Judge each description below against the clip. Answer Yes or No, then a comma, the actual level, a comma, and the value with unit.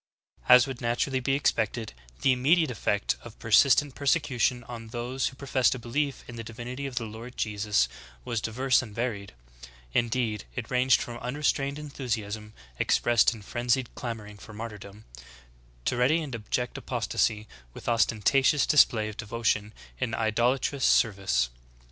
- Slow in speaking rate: No, average, 155 wpm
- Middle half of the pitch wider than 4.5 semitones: No, average, 3.1 semitones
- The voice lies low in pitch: Yes, low, 120 Hz